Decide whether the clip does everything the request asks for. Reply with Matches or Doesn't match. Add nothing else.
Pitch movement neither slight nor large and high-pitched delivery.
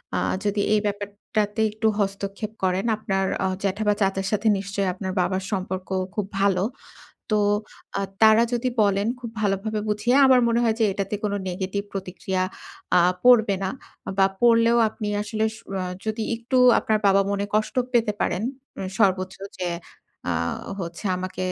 Doesn't match